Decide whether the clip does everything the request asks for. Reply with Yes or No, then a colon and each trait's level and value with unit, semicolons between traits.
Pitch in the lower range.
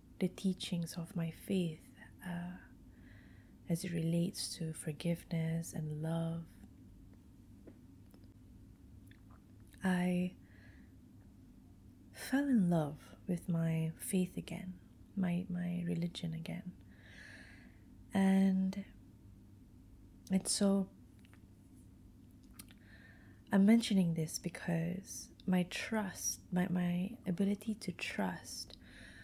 No: medium, 170 Hz